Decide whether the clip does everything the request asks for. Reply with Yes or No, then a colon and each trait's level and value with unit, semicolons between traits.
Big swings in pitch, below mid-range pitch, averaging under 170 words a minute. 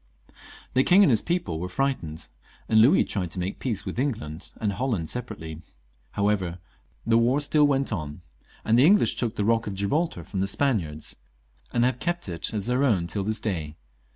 No: wide, 6.7 semitones; low, 110 Hz; average, 190 wpm